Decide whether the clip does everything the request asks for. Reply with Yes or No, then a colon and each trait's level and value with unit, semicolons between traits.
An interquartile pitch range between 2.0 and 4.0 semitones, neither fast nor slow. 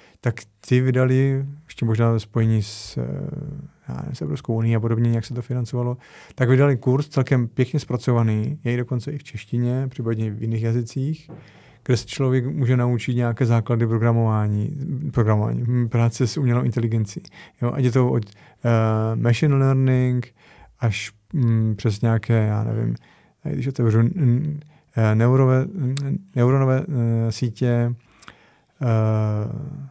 Yes: narrow, 2.5 semitones; average, 135 wpm